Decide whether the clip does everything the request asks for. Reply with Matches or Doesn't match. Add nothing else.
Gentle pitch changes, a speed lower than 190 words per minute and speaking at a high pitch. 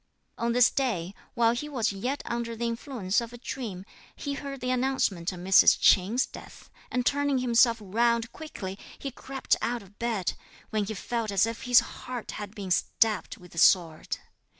Doesn't match